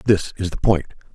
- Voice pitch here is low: Yes, very low, 95 Hz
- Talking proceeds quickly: Yes, fast, 210 wpm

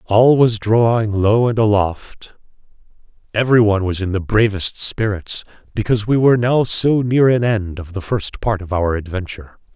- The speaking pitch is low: Yes, low, 105 Hz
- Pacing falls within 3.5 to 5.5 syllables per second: Yes, 5.0 syllables/s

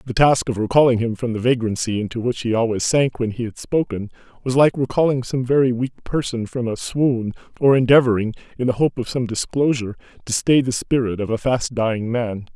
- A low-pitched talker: Yes, low, 120 Hz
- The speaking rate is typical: No, fast, 210 wpm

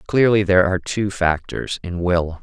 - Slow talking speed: No, average, 175 wpm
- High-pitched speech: No, very low, 95 Hz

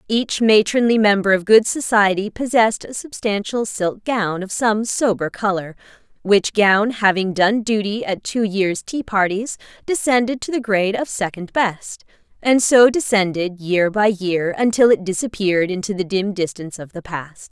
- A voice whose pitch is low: No, high, 205 Hz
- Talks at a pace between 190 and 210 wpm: No, average, 165 wpm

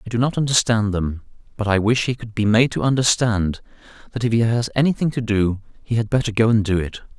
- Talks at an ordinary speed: No, fast, 235 wpm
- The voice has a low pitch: Yes, low, 110 Hz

